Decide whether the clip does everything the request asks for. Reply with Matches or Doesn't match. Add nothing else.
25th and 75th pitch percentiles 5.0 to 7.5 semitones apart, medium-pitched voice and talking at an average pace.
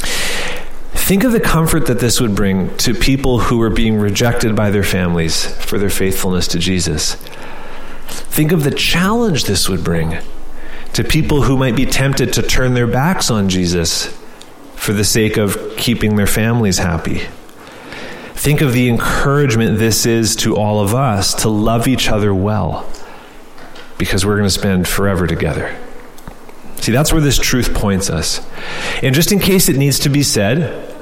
Doesn't match